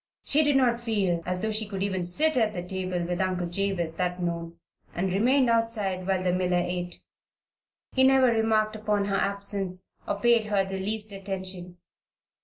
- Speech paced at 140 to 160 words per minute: No, average, 180 wpm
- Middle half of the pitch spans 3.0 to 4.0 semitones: Yes, average, 3.3 semitones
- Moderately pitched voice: No, high, 195 Hz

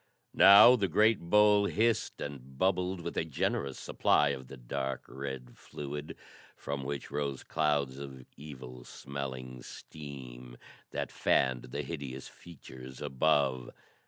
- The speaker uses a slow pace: Yes, slow, 130 wpm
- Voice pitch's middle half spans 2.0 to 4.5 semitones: Yes, average, 3.4 semitones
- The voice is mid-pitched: No, very low, 70 Hz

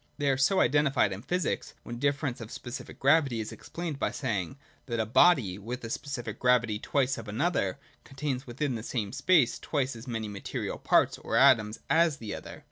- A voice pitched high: No, low, 125 Hz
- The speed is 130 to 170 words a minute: No, average, 200 wpm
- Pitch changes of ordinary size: Yes, average, 4.0 semitones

